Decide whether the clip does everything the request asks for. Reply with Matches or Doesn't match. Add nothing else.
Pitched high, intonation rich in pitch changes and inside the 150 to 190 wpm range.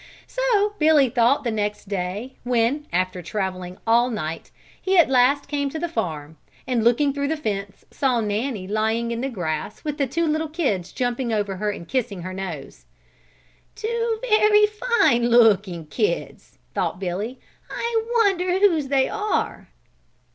Matches